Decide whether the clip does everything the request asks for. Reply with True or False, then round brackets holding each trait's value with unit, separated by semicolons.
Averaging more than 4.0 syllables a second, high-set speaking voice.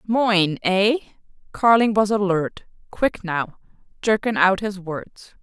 False (3.8 syllables/s; 200 Hz)